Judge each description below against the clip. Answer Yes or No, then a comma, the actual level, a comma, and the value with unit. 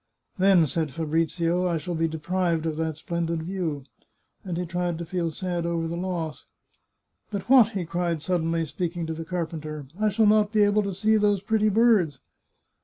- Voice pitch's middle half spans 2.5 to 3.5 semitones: Yes, average, 3.0 semitones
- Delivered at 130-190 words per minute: No, fast, 205 wpm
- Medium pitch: Yes, medium, 170 Hz